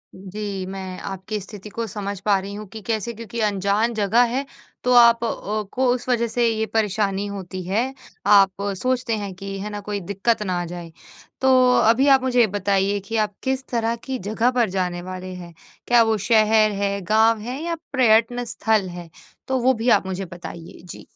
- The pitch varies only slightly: No, average, 3.3 semitones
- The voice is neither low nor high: No, high, 210 Hz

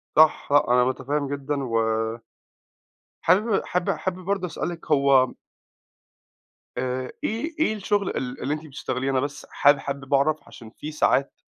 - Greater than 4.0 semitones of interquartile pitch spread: Yes, average, 4.8 semitones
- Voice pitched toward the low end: No, medium, 145 Hz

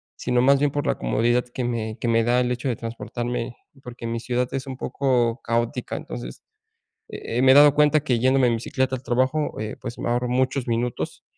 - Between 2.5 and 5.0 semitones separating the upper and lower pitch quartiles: No, narrow, 1.9 semitones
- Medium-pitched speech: No, low, 125 Hz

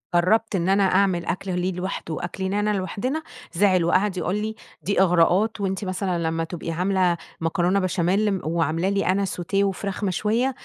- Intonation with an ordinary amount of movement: No, narrow, 2.3 semitones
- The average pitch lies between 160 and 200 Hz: Yes, high, 190 Hz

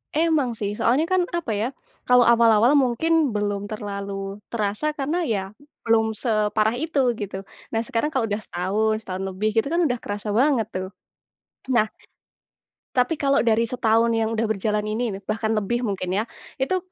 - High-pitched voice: Yes, high, 225 Hz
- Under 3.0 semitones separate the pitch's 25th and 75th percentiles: No, average, 3.3 semitones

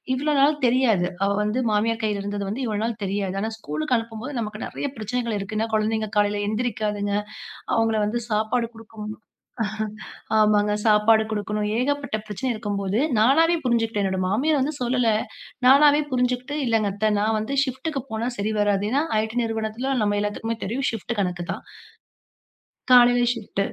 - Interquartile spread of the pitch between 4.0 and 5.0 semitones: No, average, 2.9 semitones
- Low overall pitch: No, high, 220 Hz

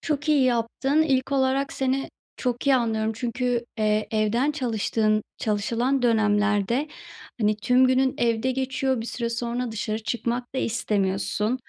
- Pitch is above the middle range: Yes, high, 240 Hz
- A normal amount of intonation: Yes, average, 3.2 semitones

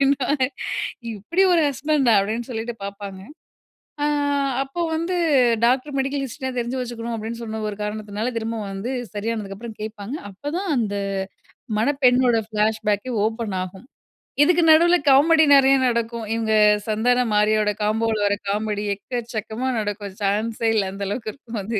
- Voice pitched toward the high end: Yes, high, 230 Hz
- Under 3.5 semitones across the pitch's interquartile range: No, average, 3.8 semitones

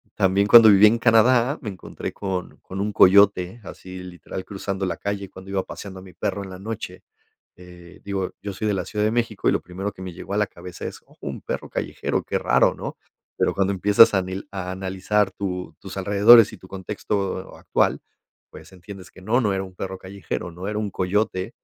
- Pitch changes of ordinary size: No, narrow, 1.9 semitones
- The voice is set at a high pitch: No, very low, 95 Hz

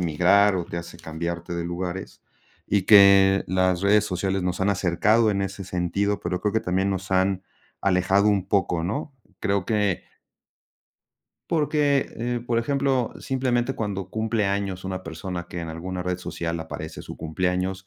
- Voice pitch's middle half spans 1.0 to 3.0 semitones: Yes, narrow, 2.6 semitones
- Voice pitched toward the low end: Yes, very low, 95 Hz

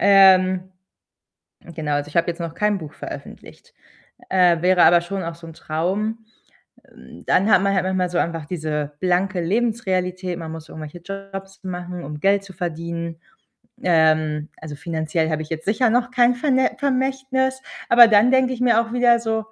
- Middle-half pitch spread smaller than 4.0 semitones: No, average, 5.0 semitones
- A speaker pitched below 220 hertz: Yes, medium, 185 Hz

